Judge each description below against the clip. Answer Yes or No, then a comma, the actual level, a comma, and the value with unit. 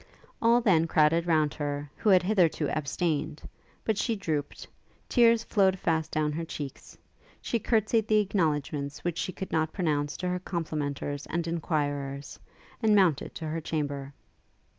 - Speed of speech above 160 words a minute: No, average, 150 wpm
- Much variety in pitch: No, average, 4.3 semitones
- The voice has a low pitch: No, medium, 160 Hz